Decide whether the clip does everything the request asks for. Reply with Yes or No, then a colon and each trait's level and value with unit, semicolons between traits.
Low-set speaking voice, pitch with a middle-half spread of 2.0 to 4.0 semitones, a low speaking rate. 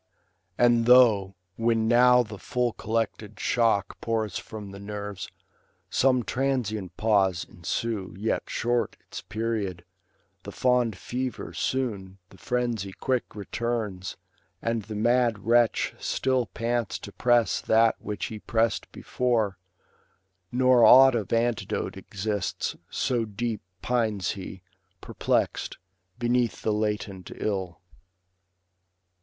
Yes: low, 115 Hz; average, 3.0 semitones; slow, 115 wpm